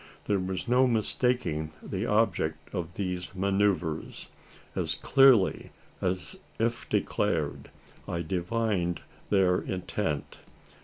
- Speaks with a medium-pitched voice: No, very low, 95 Hz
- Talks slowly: Yes, slow, 100 wpm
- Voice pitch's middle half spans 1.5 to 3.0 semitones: No, average, 3.9 semitones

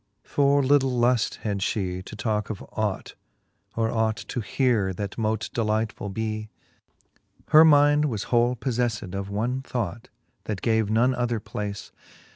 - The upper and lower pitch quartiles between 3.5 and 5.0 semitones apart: No, average, 3.0 semitones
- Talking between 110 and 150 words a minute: Yes, average, 145 wpm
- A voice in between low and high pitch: No, low, 110 Hz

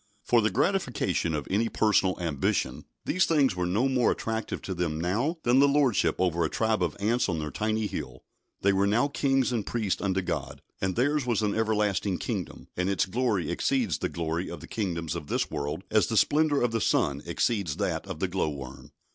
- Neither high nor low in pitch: No, low, 105 Hz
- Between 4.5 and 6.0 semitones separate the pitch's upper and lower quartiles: Yes, wide, 5.5 semitones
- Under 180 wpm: No, fast, 205 wpm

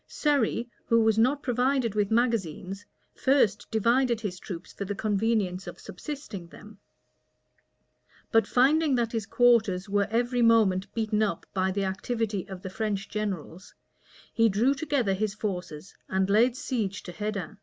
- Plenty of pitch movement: No, average, 3.5 semitones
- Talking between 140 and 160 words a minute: Yes, average, 150 wpm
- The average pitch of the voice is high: Yes, high, 215 Hz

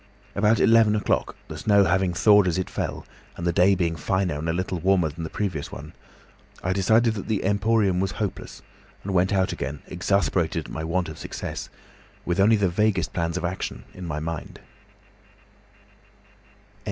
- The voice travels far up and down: No, average, 3.1 semitones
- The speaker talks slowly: No, average, 175 wpm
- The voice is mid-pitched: No, very low, 95 Hz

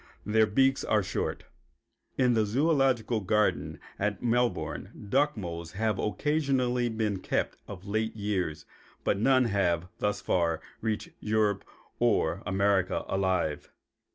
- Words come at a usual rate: No, slow, 125 wpm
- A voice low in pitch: Yes, low, 105 Hz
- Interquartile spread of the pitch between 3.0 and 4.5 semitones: Yes, average, 4.0 semitones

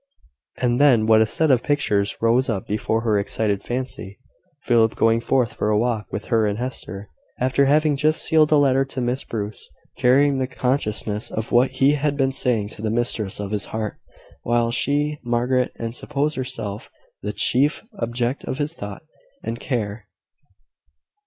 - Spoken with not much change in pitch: No, average, 3.9 semitones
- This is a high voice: No, low, 120 Hz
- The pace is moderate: Yes, average, 170 wpm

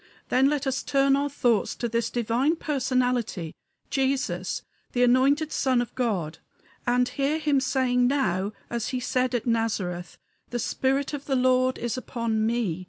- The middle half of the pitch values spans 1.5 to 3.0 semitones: Yes, average, 2.7 semitones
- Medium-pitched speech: No, very high, 250 Hz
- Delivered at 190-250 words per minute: No, average, 160 wpm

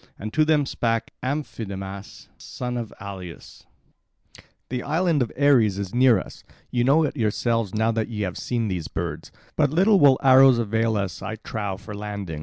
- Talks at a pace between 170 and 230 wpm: Yes, average, 175 wpm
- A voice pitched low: Yes, low, 115 Hz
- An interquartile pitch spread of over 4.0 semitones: Yes, average, 4.6 semitones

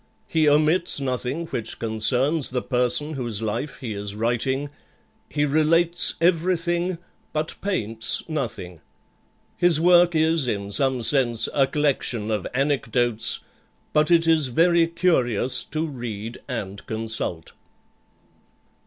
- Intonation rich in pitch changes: Yes, wide, 5.9 semitones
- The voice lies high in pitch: No, low, 135 Hz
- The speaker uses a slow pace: Yes, slow, 120 wpm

